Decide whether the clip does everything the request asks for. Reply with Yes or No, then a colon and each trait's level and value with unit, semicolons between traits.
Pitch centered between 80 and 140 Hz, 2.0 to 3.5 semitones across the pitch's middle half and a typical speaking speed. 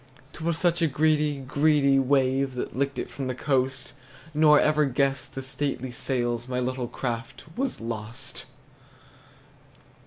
Yes: low, 135 Hz; average, 2.7 semitones; average, 145 wpm